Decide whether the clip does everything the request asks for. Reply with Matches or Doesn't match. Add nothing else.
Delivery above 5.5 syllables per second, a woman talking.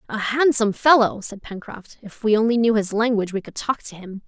Matches